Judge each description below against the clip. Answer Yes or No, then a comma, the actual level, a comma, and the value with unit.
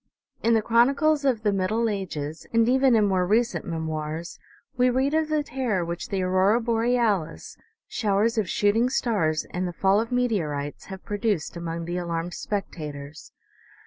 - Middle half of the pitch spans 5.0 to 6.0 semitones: Yes, wide, 5.5 semitones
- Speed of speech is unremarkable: Yes, average, 160 wpm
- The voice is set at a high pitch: Yes, high, 205 Hz